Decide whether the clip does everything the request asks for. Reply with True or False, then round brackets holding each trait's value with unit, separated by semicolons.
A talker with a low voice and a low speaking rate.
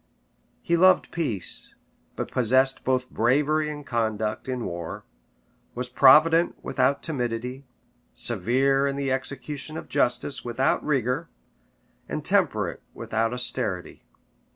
True (130 Hz; 110 wpm)